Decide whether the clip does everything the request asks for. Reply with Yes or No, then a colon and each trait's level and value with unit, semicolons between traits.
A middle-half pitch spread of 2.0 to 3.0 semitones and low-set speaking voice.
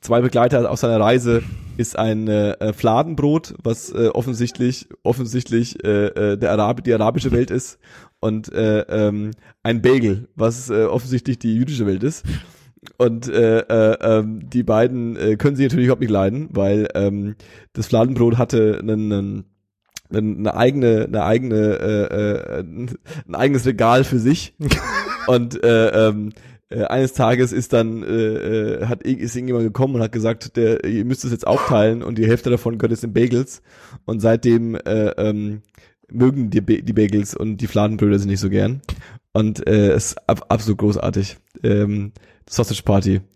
Yes: narrow, 2.4 semitones; low, 115 Hz